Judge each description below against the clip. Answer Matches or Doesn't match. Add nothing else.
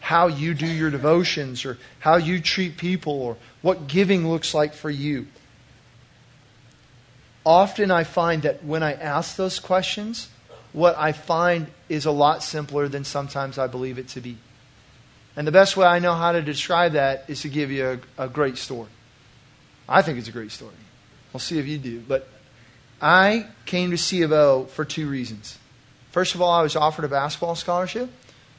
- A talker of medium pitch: Matches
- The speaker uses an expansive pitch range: Doesn't match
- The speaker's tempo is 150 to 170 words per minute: Doesn't match